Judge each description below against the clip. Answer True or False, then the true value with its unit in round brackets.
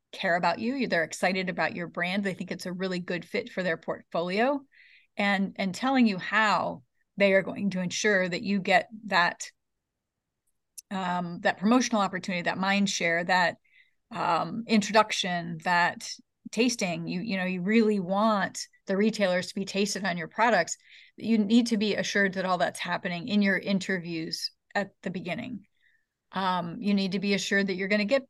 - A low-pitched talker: False (195 Hz)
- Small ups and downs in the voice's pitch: False (3.0 semitones)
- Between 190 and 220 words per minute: False (180 wpm)